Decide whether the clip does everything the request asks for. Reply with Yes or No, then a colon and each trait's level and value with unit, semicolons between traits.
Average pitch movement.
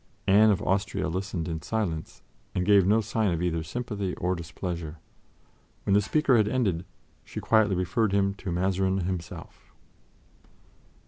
Yes: average, 3.0 semitones